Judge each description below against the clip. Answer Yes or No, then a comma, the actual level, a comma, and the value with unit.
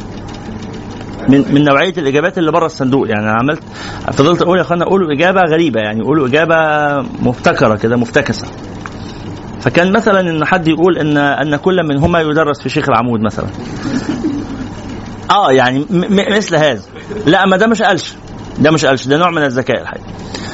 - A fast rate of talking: Yes, fast, 165 wpm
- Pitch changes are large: Yes, wide, 7.3 semitones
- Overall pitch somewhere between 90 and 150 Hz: Yes, medium, 140 Hz